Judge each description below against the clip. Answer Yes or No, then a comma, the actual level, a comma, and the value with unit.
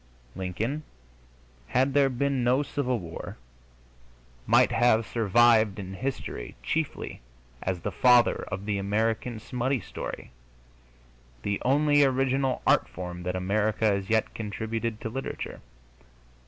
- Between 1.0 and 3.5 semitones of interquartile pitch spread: No, average, 4.6 semitones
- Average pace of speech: No, slow, 120 wpm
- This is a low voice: Yes, low, 115 Hz